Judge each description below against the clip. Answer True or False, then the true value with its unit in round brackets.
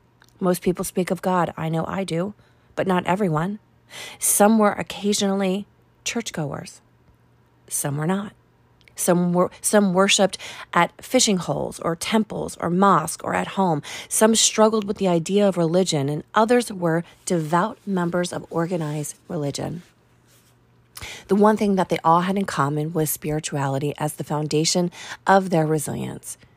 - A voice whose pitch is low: False (180 Hz)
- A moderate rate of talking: True (145 wpm)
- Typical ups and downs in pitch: True (3.6 semitones)